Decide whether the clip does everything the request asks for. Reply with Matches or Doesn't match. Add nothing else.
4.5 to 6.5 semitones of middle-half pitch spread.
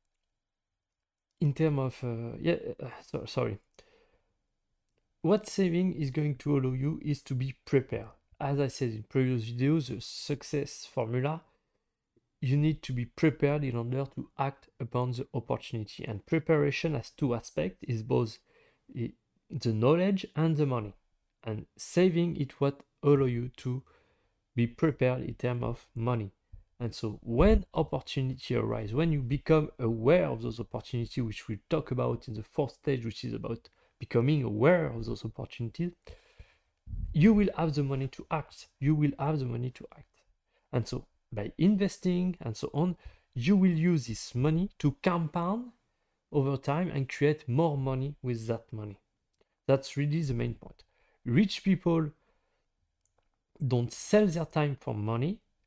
Matches